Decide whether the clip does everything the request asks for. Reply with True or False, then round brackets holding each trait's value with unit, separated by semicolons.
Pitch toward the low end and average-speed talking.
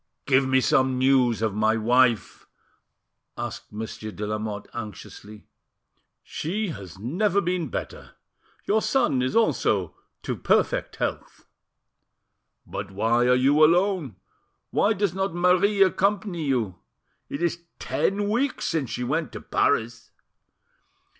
False (130 Hz; 125 wpm)